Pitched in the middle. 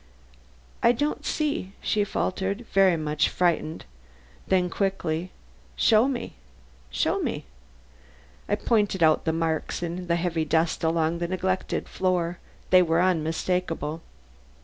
Yes: medium, 180 Hz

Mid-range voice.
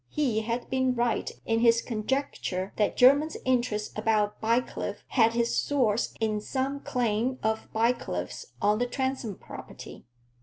No: high, 230 Hz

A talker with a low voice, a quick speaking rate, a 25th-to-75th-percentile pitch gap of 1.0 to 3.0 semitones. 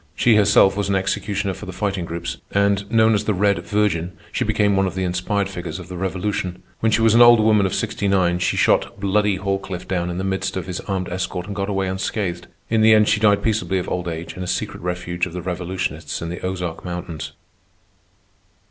Yes: very low, 95 Hz; fast, 225 wpm; narrow, 2.4 semitones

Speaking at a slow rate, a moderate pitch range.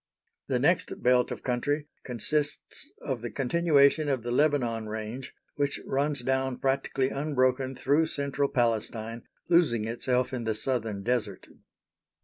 Yes: slow, 130 wpm; average, 3.3 semitones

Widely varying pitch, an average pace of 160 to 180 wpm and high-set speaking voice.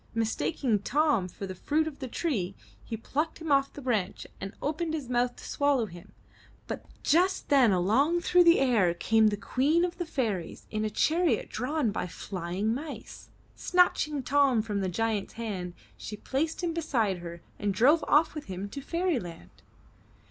Yes: wide, 7.1 semitones; average, 175 wpm; very high, 250 Hz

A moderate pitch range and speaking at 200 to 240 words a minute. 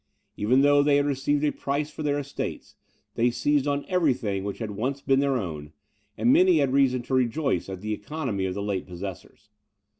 No: wide, 5.7 semitones; fast, 205 wpm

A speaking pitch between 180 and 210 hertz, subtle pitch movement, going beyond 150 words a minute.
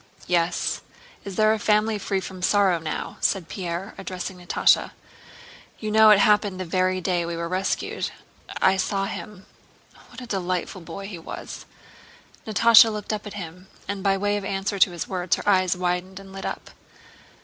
Yes: high, 190 Hz; narrow, 2.3 semitones; average, 170 wpm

